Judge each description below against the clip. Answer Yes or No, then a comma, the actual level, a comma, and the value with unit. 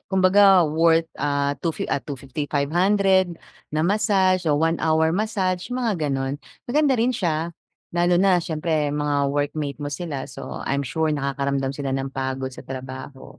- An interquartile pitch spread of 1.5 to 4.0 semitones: No, average, 4.7 semitones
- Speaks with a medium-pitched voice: Yes, medium, 160 Hz